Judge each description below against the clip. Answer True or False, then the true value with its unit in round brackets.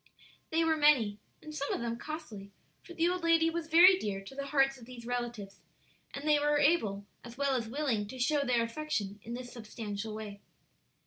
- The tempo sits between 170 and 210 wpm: True (200 wpm)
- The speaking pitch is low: False (255 Hz)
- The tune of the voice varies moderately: False (5.7 semitones)